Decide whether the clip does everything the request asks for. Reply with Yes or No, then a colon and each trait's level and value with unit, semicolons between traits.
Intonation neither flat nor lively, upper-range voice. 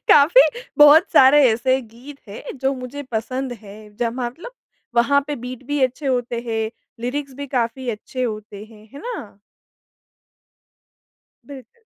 Yes: average, 3.6 semitones; very high, 255 Hz